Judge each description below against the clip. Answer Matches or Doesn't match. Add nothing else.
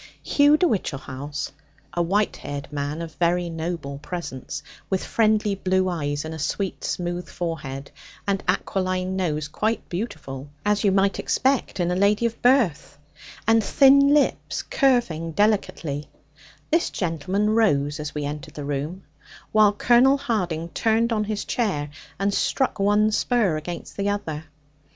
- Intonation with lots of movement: Matches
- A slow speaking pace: Doesn't match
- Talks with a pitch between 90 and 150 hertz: Doesn't match